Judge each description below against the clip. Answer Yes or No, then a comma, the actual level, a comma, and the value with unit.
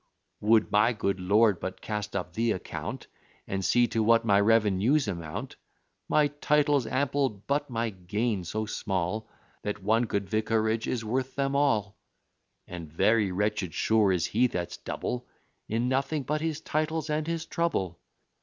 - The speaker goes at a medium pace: Yes, average, 155 wpm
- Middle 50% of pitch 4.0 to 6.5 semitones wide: Yes, average, 4.9 semitones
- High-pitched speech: No, low, 110 Hz